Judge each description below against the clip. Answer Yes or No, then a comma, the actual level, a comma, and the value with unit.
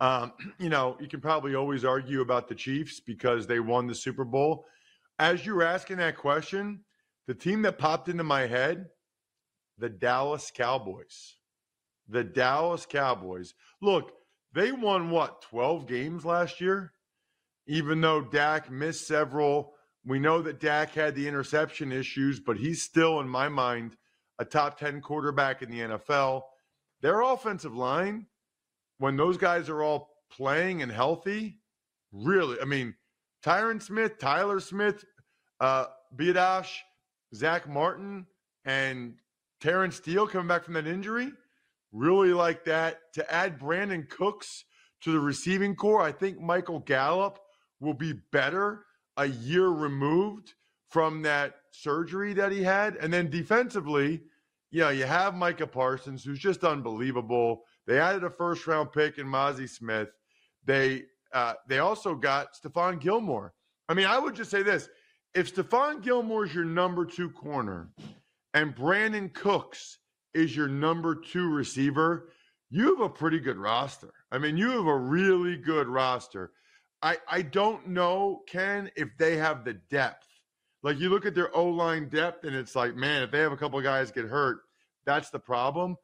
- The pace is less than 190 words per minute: Yes, average, 155 wpm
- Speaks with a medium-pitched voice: Yes, medium, 160 Hz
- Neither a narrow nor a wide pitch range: Yes, average, 5.0 semitones